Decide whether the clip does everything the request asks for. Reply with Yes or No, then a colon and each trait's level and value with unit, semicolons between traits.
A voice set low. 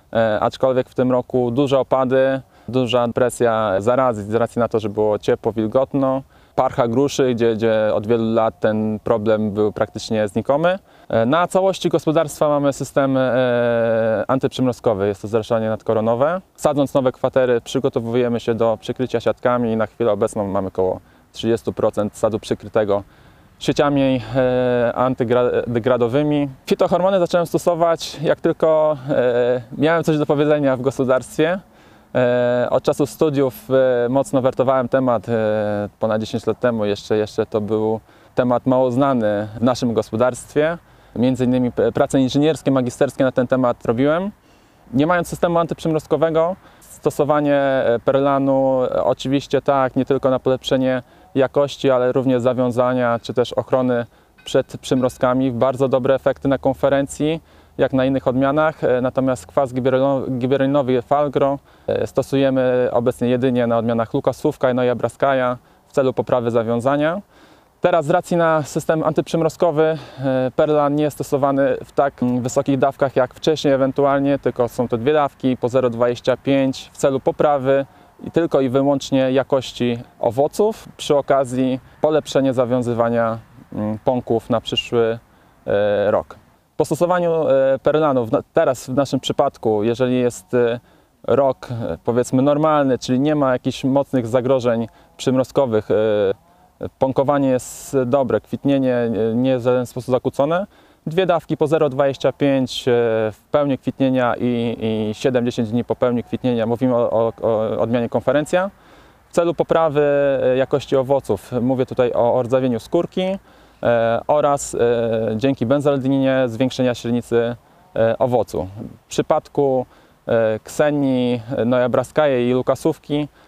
Yes: low, 130 Hz